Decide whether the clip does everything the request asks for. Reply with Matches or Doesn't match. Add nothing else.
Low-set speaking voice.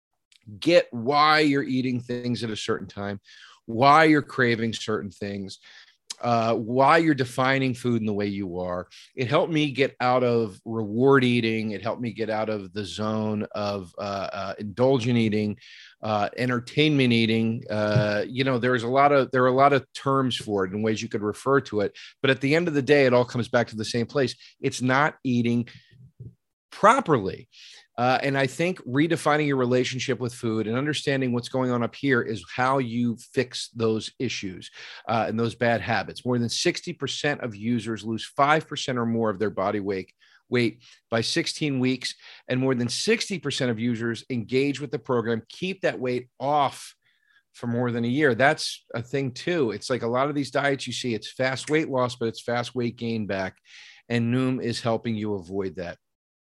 Matches